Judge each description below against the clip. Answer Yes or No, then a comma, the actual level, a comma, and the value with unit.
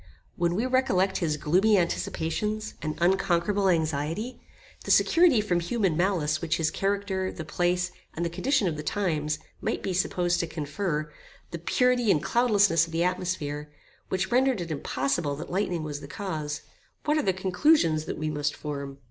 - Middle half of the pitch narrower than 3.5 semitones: No, average, 4.5 semitones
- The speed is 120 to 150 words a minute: No, average, 170 wpm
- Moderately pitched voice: Yes, medium, 175 Hz